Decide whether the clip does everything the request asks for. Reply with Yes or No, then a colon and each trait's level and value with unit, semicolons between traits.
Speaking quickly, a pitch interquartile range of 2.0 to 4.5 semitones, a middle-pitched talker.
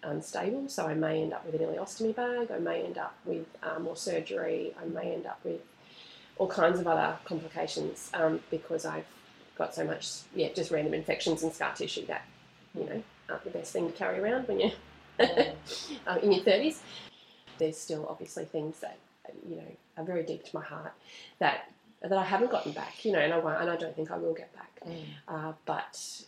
Yes: fast, 210 wpm; average, 3.5 semitones; medium, 165 Hz